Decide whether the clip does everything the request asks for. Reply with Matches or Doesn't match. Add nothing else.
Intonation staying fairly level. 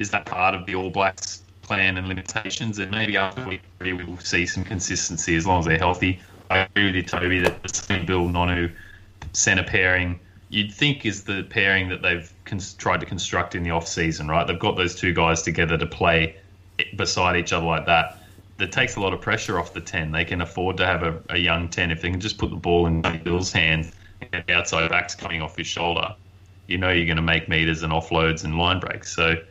Matches